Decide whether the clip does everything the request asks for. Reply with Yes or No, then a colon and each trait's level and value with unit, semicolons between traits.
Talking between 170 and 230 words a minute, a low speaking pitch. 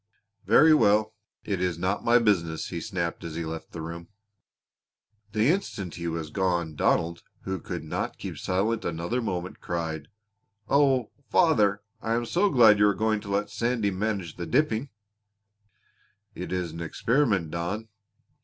No: average, 155 wpm; low, 100 Hz